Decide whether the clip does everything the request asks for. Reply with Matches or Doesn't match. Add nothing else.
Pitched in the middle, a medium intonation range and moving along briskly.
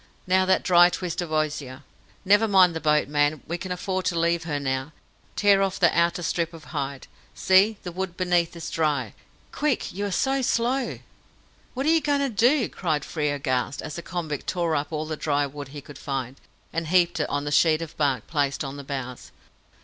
Matches